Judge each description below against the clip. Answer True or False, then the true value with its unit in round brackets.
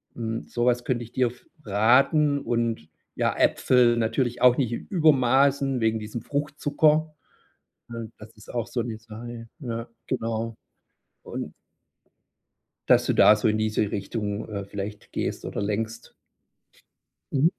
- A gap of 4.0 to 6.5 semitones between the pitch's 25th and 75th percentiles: False (2.8 semitones)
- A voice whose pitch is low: True (115 Hz)